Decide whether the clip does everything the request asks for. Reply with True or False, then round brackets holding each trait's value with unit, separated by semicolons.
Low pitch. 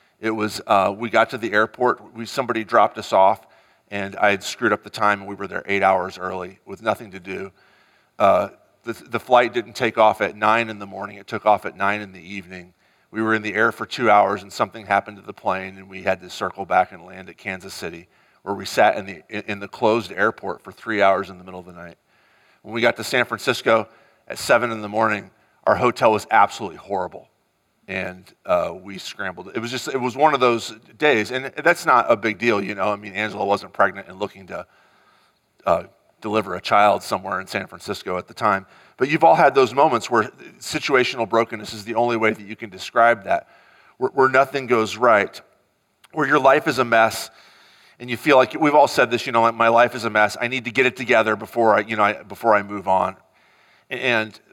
True (110 Hz)